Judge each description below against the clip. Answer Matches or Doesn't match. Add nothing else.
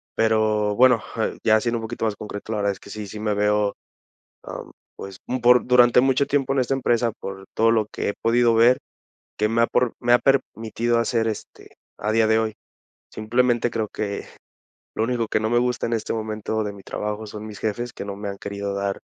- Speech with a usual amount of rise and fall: Doesn't match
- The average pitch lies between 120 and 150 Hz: Doesn't match